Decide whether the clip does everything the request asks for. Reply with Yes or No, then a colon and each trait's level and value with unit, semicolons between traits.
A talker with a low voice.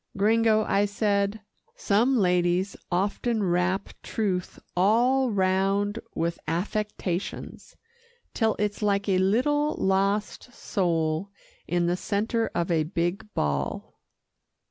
No: high, 200 Hz